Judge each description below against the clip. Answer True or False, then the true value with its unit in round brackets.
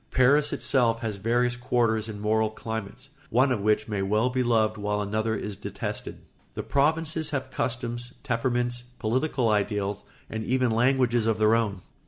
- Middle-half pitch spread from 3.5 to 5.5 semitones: False (2.8 semitones)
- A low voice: True (115 Hz)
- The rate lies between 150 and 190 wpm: True (160 wpm)